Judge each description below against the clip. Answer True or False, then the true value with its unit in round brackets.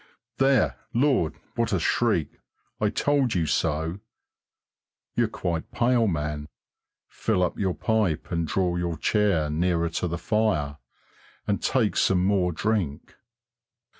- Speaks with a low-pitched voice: True (90 Hz)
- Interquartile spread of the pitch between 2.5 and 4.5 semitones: False (5.1 semitones)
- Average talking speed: False (130 wpm)